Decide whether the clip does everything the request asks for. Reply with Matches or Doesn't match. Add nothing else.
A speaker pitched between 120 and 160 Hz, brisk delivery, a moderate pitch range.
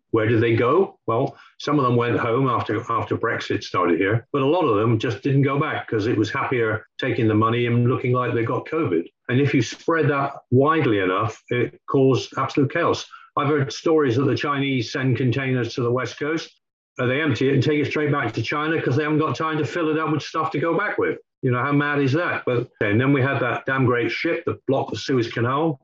Matches